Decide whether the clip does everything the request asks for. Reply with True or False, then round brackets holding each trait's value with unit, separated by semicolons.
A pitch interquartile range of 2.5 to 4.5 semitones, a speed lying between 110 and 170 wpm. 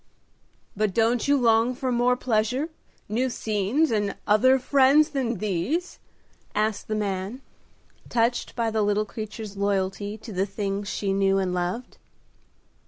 True (3.7 semitones; 140 wpm)